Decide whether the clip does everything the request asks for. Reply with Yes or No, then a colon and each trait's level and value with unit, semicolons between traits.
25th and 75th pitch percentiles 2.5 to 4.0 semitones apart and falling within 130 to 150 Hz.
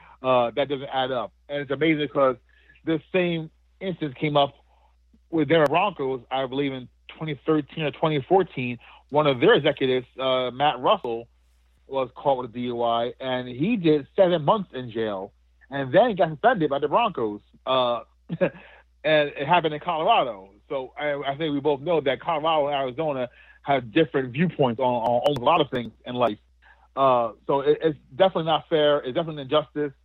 Yes: average, 3.6 semitones; medium, 140 Hz